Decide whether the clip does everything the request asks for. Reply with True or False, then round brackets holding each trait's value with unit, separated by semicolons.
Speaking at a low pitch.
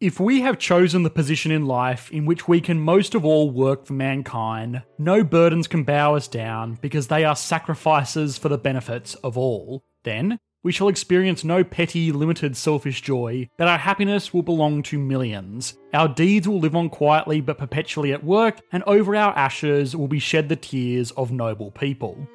False (150 Hz)